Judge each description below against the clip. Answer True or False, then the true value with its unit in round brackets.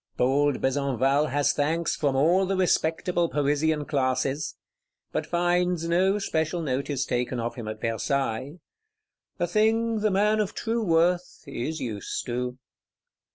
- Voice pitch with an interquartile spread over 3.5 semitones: True (5.0 semitones)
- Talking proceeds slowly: True (130 wpm)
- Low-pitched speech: False (155 Hz)